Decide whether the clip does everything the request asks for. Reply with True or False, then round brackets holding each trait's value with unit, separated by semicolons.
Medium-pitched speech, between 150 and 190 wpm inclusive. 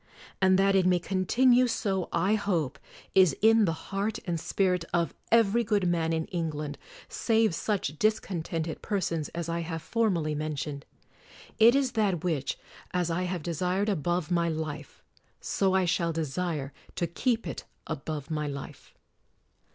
True (175 Hz; 155 wpm)